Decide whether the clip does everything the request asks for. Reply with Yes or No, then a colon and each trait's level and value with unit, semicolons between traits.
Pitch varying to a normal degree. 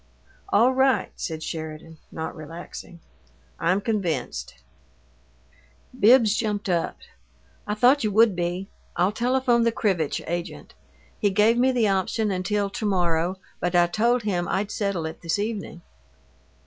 Yes: average, 4.6 semitones